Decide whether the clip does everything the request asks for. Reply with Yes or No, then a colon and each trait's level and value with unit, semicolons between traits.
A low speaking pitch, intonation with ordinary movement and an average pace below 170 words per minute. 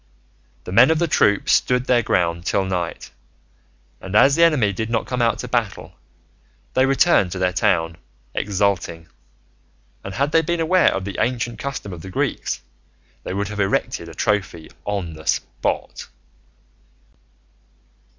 No: low, 100 Hz; wide, 5.8 semitones; average, 155 wpm